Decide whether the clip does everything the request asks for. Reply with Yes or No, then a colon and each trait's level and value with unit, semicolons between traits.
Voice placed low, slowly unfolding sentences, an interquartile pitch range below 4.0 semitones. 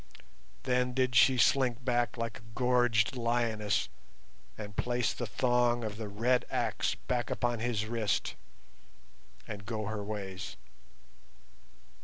Yes: low, 120 Hz; slow, 125 wpm; narrow, 2.4 semitones